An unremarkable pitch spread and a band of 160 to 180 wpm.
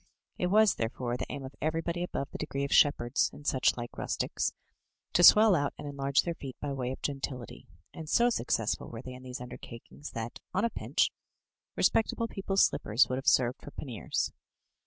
No: average, 4.8 semitones; average, 190 wpm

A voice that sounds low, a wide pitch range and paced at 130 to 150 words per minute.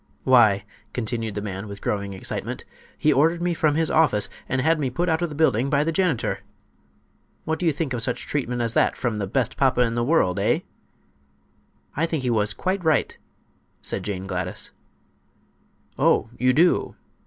No: low, 130 Hz; wide, 6.6 semitones; average, 185 wpm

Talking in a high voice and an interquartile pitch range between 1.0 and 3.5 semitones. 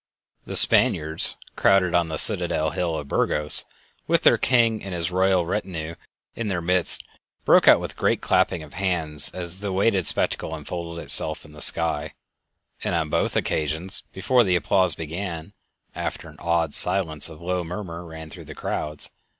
No: very low, 85 Hz; average, 3.0 semitones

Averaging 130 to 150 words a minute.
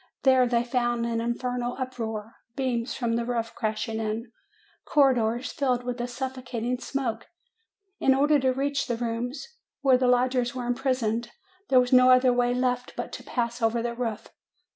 No: average, 165 wpm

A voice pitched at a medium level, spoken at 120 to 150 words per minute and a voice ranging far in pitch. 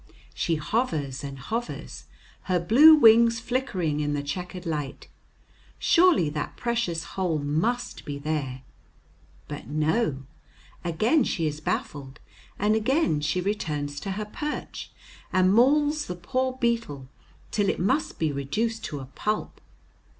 Yes: medium, 180 Hz; slow, 135 wpm; wide, 7.9 semitones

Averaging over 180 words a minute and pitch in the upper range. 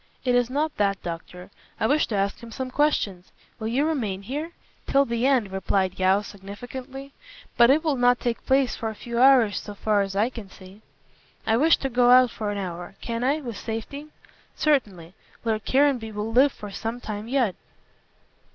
Yes: average, 190 wpm; high, 230 Hz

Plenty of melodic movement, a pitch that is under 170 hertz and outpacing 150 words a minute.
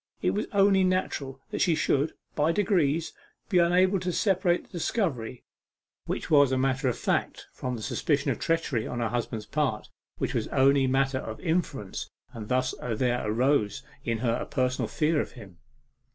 Yes: wide, 5.7 semitones; low, 135 Hz; average, 170 wpm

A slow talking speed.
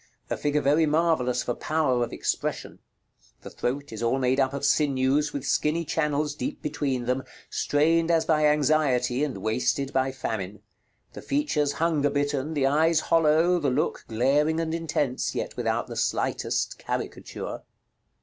No: average, 155 wpm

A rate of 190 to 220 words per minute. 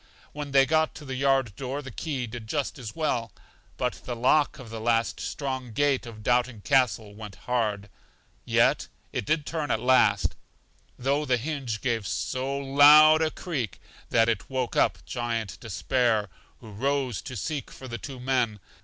No: average, 170 wpm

